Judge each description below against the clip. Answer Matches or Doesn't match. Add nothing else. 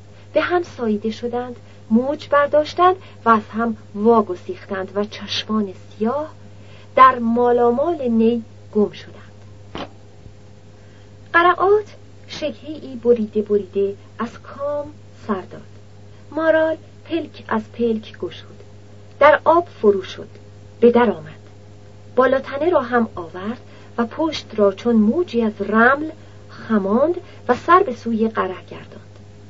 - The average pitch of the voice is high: Matches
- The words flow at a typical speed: Matches